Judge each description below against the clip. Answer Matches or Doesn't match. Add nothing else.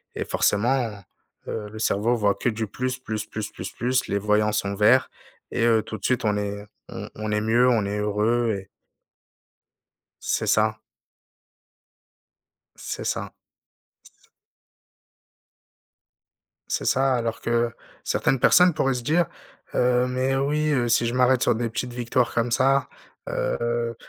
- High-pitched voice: Doesn't match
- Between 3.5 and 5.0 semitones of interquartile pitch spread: Doesn't match